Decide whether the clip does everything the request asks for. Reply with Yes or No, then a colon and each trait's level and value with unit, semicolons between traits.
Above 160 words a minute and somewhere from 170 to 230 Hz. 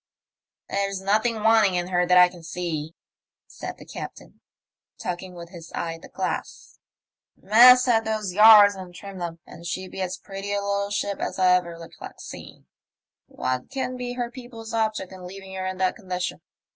Yes: average, 185 wpm; high, 190 Hz